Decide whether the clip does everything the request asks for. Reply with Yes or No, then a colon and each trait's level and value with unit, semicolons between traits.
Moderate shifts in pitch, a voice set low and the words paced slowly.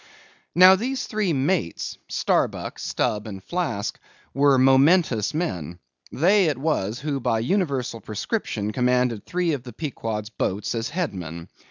No: wide, 8.1 semitones; low, 130 Hz; slow, 130 wpm